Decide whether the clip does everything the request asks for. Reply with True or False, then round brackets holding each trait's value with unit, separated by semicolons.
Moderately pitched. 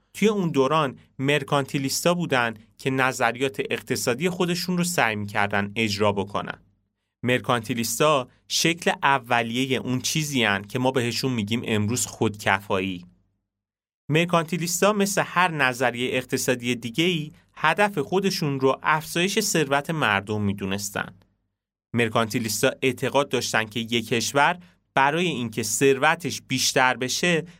False (130 Hz)